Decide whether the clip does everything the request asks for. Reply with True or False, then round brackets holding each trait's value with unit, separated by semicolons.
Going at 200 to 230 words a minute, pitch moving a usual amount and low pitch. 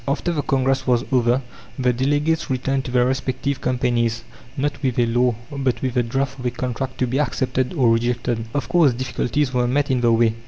False (205 wpm; 2.0 semitones; 130 Hz)